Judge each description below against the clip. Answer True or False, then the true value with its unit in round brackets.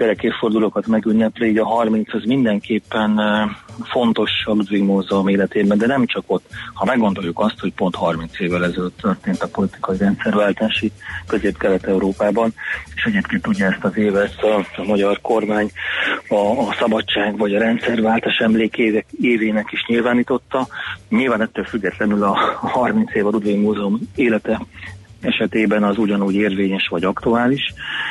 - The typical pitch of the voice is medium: False (105 Hz)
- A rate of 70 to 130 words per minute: False (140 wpm)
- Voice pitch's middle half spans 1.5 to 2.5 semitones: True (1.9 semitones)